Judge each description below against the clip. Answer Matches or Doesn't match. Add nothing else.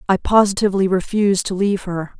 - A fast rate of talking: Doesn't match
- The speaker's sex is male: Doesn't match